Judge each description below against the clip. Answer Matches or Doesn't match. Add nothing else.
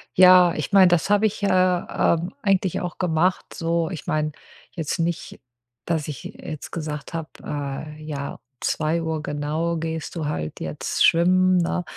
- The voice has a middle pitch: Matches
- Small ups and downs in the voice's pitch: Doesn't match